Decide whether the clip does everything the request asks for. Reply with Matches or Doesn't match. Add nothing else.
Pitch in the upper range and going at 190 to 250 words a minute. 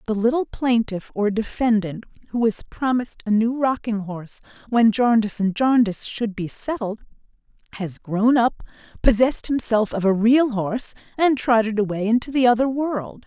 Doesn't match